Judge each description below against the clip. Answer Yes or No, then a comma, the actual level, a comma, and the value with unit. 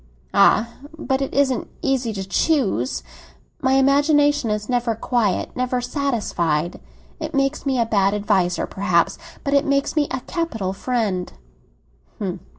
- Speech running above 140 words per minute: No, slow, 135 wpm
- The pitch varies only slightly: No, average, 5.1 semitones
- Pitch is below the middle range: No, very high, 250 Hz